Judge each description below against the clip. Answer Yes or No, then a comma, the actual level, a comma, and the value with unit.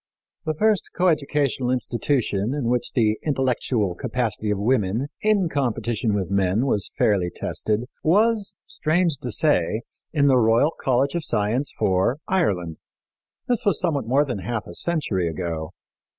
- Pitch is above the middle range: No, low, 125 Hz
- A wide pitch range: Yes, wide, 6.3 semitones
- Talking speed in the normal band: Yes, average, 145 wpm